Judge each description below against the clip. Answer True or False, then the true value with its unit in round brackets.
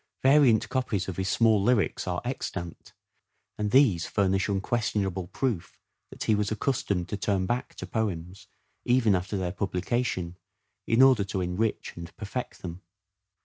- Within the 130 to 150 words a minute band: True (145 wpm)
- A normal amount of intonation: True (4.0 semitones)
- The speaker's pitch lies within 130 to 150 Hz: False (100 Hz)